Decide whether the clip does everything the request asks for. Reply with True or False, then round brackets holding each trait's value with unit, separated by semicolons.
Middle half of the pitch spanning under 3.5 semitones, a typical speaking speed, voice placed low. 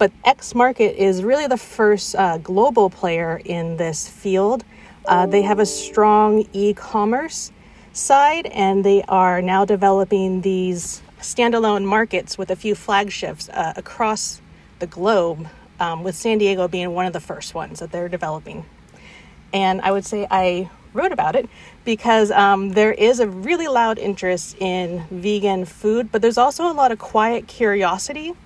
False (3.1 semitones; 160 wpm; 200 Hz)